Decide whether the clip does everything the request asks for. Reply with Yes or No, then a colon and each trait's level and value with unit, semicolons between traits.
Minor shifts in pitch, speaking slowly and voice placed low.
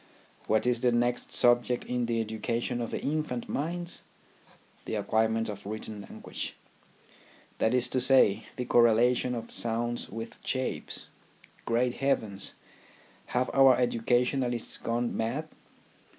Yes: narrow, 1.8 semitones; slow, 130 wpm; low, 120 Hz